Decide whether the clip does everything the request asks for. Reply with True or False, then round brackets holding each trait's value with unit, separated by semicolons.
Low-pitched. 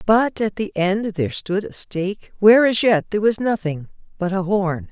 False (195 Hz)